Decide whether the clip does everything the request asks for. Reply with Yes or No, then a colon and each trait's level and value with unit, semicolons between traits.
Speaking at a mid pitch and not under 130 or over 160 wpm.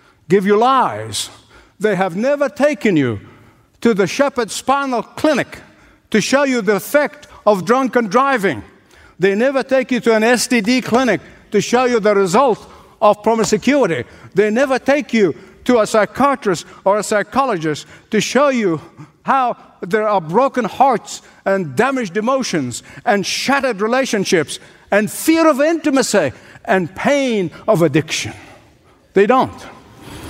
No: high, 220 Hz; average, 140 wpm